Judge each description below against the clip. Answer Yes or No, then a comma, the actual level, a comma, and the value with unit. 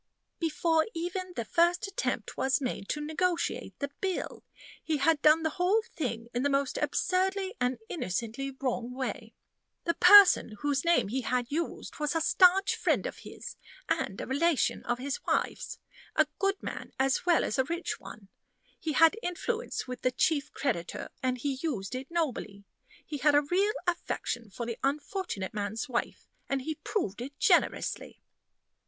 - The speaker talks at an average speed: Yes, average, 165 wpm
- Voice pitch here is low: No, very high, 290 Hz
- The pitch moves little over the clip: No, average, 5.3 semitones